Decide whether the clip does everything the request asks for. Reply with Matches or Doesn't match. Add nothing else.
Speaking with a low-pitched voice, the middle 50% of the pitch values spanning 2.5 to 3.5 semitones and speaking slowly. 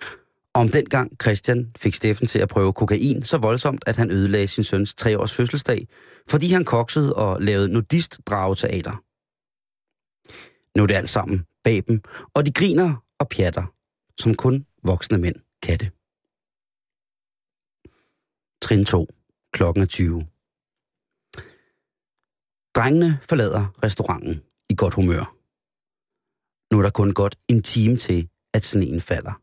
Doesn't match